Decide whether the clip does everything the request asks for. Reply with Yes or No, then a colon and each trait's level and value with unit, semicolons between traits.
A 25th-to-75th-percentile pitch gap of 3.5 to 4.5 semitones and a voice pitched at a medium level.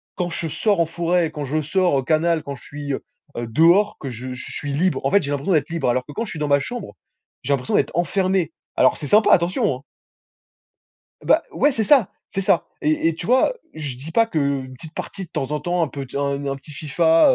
Yes: average, 4.2 semitones; medium, 155 Hz